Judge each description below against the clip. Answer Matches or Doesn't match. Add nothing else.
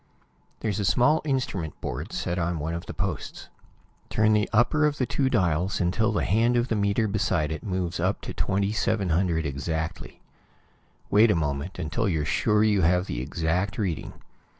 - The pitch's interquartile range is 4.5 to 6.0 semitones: Matches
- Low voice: Matches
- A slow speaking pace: Doesn't match